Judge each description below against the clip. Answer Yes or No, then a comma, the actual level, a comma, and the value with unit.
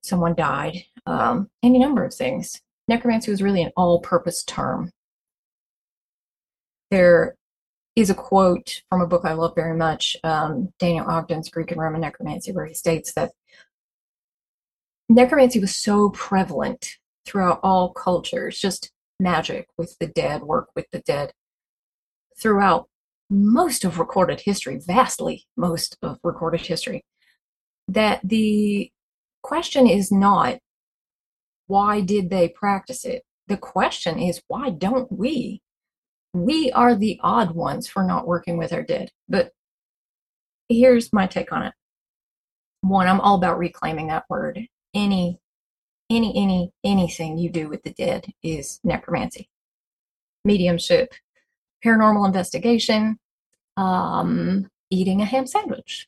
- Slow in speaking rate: Yes, slow, 130 wpm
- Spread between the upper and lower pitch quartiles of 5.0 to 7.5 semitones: Yes, average, 5.3 semitones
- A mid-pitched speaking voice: No, high, 195 Hz